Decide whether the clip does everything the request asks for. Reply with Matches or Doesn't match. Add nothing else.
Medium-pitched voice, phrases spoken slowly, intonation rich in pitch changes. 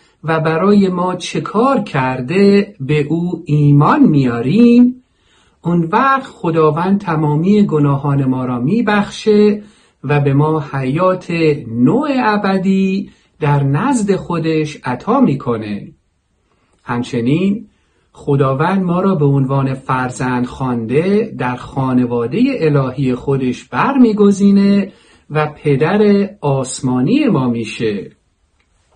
Matches